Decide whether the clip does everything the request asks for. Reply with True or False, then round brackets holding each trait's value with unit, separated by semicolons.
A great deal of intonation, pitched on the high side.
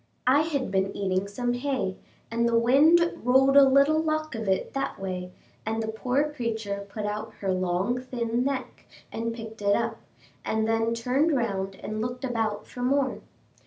False (4.3 semitones; 230 Hz)